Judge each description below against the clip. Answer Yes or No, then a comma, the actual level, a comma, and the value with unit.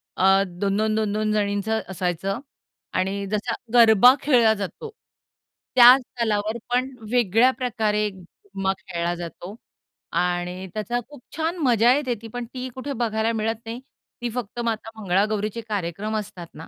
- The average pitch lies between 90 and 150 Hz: No, high, 215 Hz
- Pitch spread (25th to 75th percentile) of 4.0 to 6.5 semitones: No, average, 3.5 semitones